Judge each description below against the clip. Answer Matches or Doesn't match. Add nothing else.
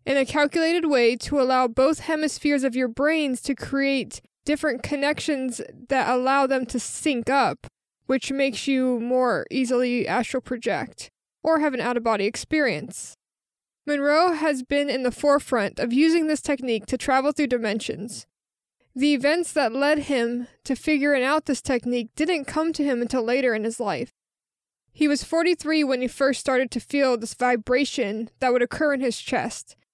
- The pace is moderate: Matches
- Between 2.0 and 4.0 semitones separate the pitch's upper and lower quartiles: Matches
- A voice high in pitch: Matches